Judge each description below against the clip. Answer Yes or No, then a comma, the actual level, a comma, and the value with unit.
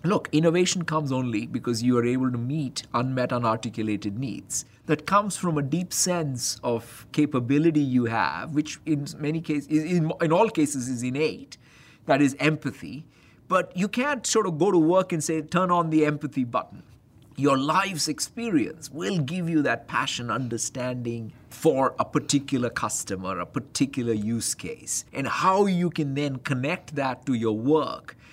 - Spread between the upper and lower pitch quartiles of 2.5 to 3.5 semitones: No, average, 4.7 semitones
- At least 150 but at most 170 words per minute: Yes, average, 165 wpm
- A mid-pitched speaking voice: Yes, medium, 145 Hz